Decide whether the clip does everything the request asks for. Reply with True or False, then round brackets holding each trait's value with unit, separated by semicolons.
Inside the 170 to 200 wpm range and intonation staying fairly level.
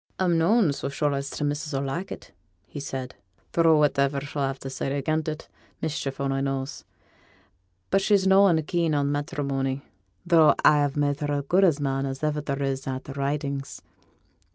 True (185 wpm; 2.3 semitones)